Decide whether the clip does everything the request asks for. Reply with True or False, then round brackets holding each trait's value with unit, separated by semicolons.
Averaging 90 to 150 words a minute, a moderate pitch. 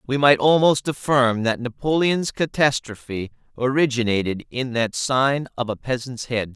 False (135 wpm; 125 Hz)